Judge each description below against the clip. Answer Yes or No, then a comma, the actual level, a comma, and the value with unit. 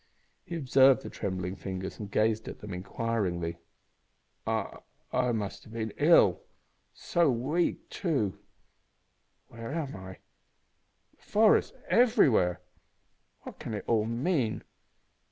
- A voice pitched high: No, low, 115 Hz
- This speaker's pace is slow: Yes, slow, 120 wpm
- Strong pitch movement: Yes, wide, 6.2 semitones